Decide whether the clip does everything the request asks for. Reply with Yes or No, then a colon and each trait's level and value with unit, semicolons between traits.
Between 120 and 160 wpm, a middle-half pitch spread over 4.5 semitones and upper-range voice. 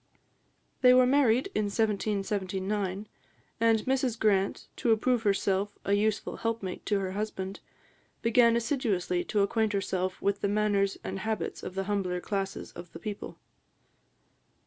No: average, 140 wpm; narrow, 2.5 semitones; high, 205 Hz